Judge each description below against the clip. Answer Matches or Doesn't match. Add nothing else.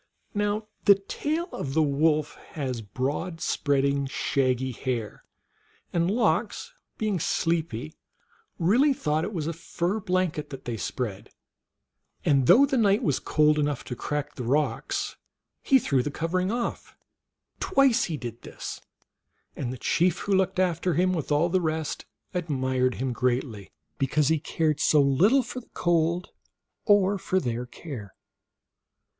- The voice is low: Doesn't match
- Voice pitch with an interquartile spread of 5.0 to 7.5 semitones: Matches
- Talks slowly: Doesn't match